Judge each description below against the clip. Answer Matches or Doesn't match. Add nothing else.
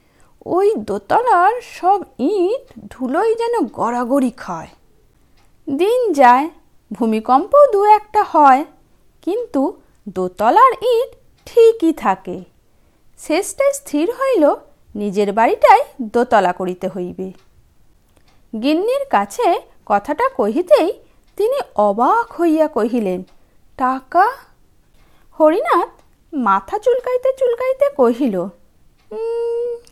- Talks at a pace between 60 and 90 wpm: Matches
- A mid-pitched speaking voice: Doesn't match